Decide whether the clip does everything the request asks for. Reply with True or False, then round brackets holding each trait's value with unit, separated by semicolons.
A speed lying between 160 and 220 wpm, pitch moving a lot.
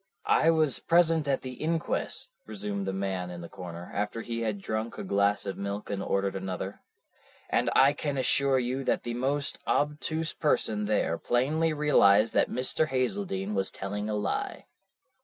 True (170 wpm; 6.5 semitones)